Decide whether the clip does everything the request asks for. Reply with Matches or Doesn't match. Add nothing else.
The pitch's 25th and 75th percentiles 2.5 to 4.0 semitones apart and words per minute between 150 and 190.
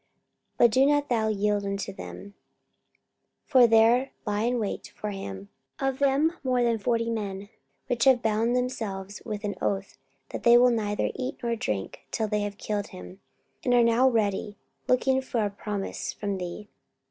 Matches